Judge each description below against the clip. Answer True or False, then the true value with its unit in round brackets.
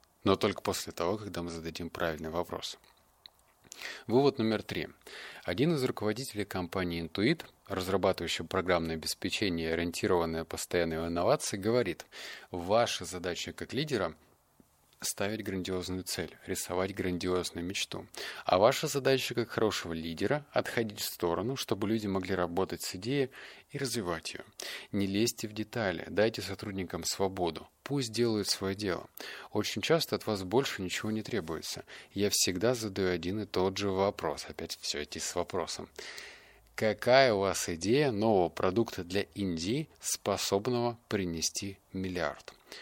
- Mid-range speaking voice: False (95 Hz)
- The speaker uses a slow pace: False (135 wpm)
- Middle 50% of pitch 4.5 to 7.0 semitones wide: False (3.6 semitones)